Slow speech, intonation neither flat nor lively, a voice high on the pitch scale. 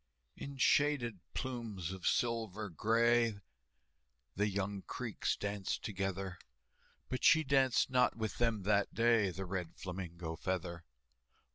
No: slow, 120 wpm; average, 4.0 semitones; low, 105 Hz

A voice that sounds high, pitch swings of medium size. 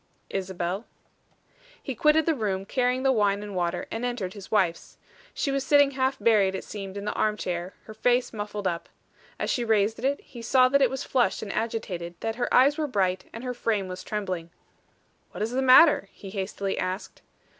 Yes: high, 215 Hz; average, 4.8 semitones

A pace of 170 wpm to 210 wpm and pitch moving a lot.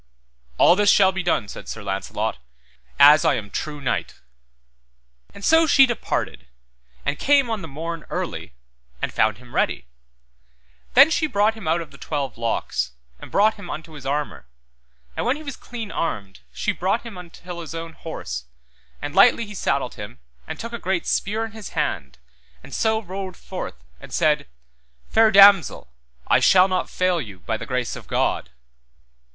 Yes: average, 175 wpm; wide, 8.9 semitones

